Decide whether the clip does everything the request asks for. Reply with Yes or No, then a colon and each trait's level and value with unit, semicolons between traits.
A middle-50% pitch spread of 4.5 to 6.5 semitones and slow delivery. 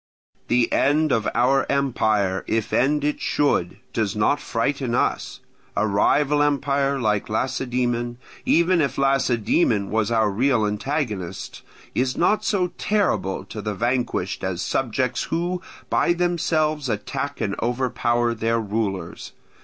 Yes: average, 4.9 semitones; slow, 130 wpm